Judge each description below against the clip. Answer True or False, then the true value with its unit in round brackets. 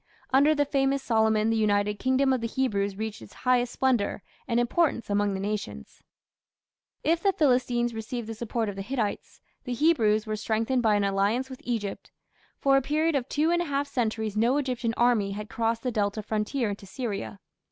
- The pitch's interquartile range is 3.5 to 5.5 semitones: True (3.8 semitones)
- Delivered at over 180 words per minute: True (190 wpm)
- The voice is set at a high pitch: True (230 Hz)